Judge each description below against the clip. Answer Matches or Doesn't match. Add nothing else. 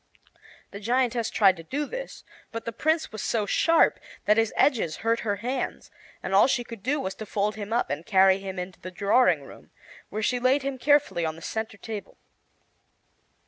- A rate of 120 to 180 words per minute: Doesn't match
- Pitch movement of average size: Matches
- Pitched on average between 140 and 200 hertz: Doesn't match